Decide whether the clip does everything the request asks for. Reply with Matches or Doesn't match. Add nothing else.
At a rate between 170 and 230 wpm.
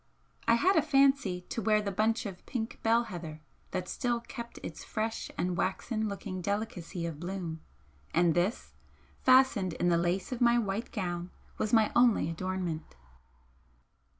Doesn't match